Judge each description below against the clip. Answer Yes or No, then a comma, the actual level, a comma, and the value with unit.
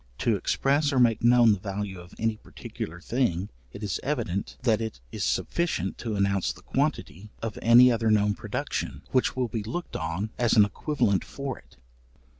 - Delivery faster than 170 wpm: Yes, average, 180 wpm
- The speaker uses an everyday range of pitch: Yes, average, 3.7 semitones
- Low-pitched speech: Yes, low, 110 Hz